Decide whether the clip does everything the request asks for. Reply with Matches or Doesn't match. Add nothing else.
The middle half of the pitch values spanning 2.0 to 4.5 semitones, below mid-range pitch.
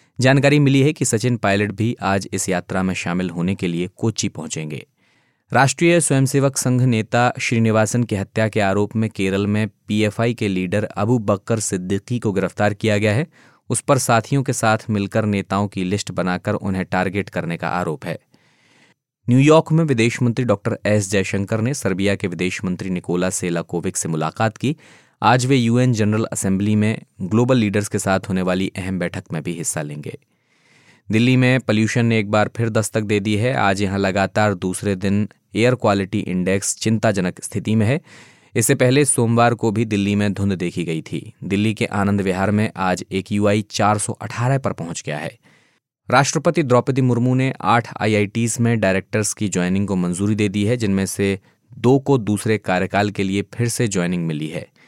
Matches